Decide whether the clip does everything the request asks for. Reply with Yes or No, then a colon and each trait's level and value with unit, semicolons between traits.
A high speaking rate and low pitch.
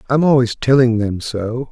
No: average, 175 wpm; low, 125 Hz